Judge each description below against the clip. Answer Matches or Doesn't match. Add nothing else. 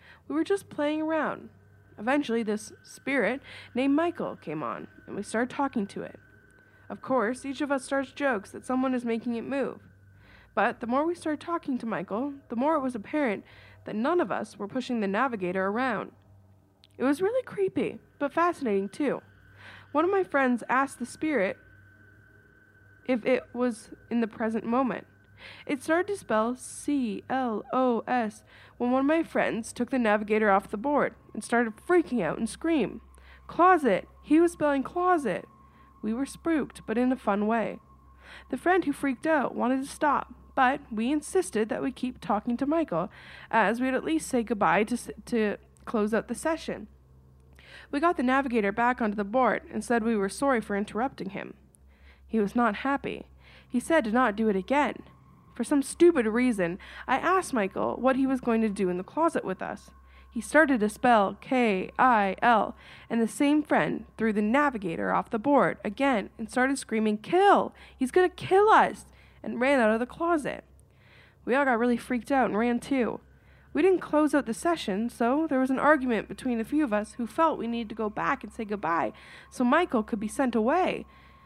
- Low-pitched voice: Doesn't match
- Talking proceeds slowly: Doesn't match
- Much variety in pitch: Doesn't match